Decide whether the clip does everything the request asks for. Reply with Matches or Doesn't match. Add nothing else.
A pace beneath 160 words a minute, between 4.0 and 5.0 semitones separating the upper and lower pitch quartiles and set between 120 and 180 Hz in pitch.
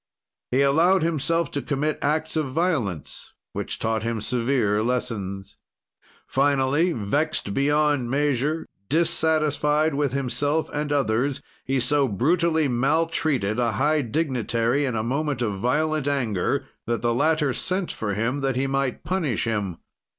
Matches